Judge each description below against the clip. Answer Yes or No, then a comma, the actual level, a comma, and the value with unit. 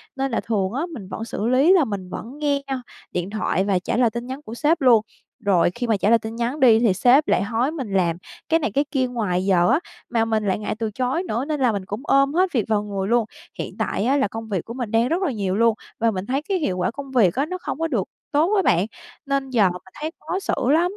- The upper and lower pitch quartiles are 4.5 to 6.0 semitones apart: Yes, average, 5.2 semitones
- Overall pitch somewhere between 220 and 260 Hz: Yes, high, 235 Hz